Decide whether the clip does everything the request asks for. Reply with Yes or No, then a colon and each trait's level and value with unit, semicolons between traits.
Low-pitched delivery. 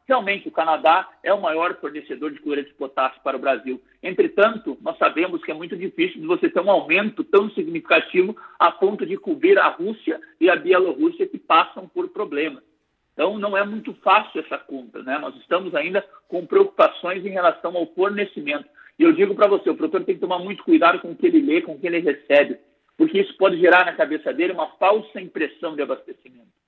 No: very high, 290 Hz